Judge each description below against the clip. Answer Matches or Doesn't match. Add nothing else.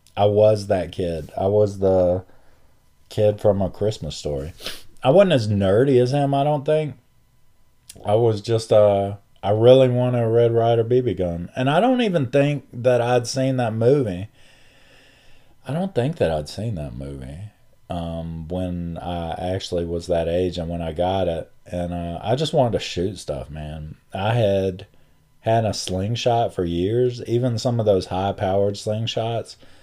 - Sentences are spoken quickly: Doesn't match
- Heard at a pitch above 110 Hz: Doesn't match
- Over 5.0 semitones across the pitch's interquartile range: Matches